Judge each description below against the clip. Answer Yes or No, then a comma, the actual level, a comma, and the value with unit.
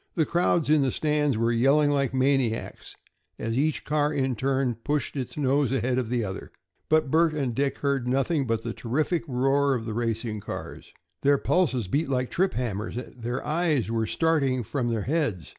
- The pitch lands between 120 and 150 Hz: Yes, low, 135 Hz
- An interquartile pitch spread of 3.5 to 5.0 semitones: Yes, average, 3.8 semitones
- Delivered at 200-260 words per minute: No, average, 185 wpm